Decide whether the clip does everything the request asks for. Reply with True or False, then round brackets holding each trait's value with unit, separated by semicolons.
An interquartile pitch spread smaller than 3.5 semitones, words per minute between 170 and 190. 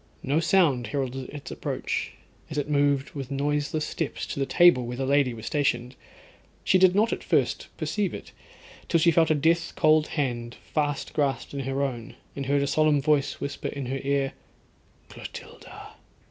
True (2.4 semitones; 175 wpm)